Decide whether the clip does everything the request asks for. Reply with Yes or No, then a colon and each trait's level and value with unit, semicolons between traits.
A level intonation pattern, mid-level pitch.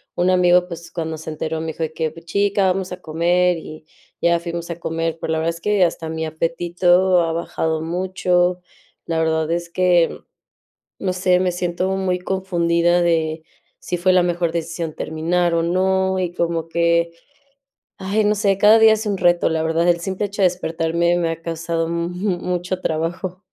Yes: narrow, 1.8 semitones; medium, 170 Hz